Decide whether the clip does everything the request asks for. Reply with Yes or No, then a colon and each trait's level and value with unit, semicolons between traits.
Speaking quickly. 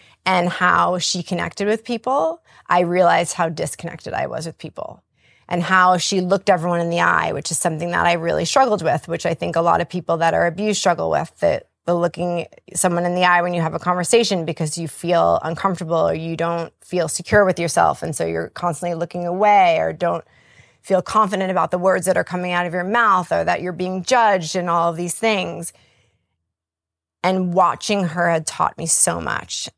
Yes: fast, 210 wpm